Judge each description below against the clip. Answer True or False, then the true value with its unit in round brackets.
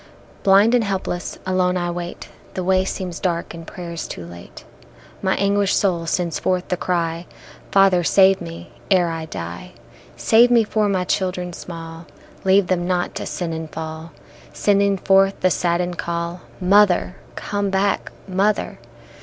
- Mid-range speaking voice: True (180 Hz)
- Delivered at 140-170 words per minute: True (155 wpm)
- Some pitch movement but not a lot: False (2.3 semitones)